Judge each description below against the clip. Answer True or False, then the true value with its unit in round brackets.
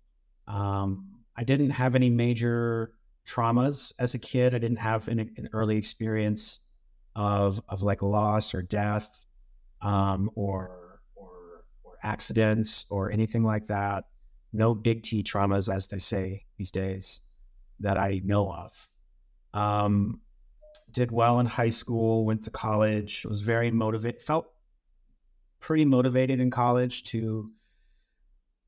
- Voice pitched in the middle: False (105 Hz)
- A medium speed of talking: False (130 wpm)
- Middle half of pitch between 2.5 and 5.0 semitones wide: True (3.0 semitones)